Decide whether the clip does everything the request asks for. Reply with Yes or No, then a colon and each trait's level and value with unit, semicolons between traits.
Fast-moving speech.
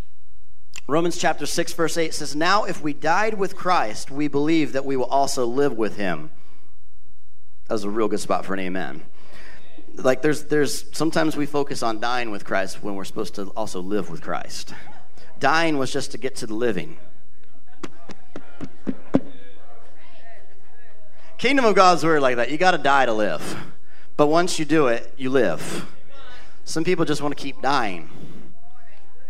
No: average, 170 wpm